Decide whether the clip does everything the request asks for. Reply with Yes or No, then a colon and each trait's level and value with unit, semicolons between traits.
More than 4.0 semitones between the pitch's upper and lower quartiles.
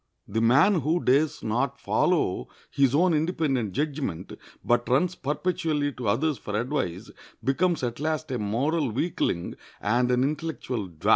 Yes: average, 4.8 semitones